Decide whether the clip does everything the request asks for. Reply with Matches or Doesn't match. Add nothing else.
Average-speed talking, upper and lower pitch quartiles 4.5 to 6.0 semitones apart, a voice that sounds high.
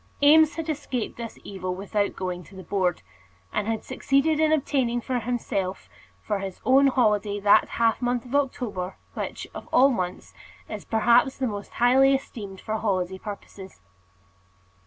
Matches